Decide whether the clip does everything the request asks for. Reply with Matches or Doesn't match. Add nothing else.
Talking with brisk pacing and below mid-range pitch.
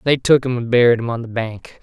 Matches